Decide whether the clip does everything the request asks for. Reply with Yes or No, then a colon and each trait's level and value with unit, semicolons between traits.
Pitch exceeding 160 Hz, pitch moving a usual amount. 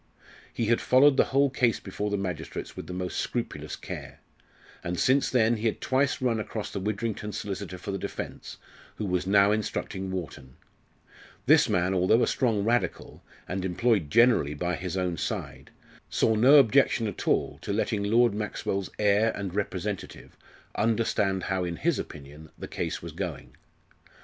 No: low, 105 Hz; average, 3.9 semitones